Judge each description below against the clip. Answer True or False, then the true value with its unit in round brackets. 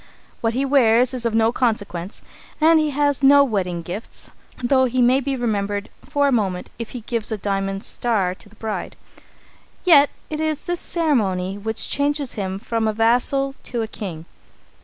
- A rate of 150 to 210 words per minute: True (180 wpm)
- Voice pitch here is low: False (230 Hz)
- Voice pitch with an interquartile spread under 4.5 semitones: False (5.2 semitones)